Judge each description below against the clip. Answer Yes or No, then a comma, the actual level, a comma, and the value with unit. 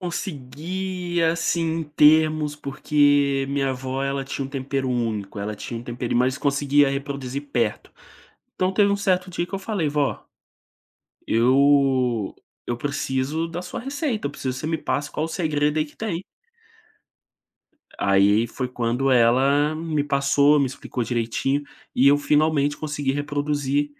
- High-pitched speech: No, medium, 145 Hz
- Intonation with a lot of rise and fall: No, average, 3.0 semitones